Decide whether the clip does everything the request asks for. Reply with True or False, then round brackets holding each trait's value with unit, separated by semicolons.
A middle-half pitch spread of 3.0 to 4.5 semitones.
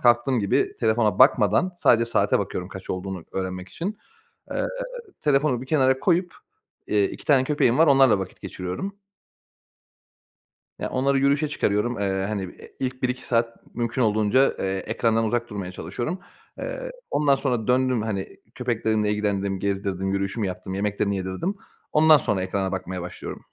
False (5.2 semitones)